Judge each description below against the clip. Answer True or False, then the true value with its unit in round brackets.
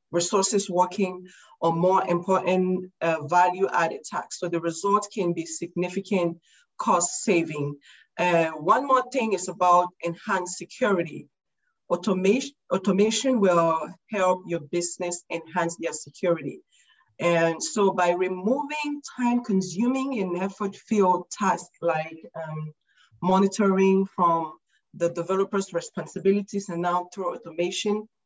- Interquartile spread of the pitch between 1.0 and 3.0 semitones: True (2.6 semitones)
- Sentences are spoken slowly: True (115 wpm)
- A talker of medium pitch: True (180 Hz)